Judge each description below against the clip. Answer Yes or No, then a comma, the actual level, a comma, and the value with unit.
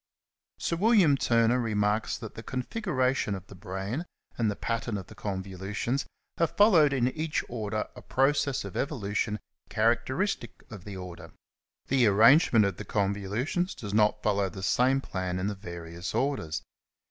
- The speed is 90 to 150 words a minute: No, average, 160 wpm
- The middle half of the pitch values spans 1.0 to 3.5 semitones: No, average, 5.1 semitones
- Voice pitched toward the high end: No, low, 110 Hz